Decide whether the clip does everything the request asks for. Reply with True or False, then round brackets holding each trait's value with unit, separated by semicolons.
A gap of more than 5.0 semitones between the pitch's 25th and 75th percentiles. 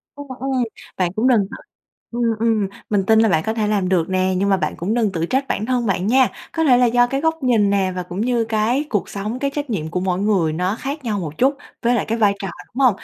False (4.5 semitones)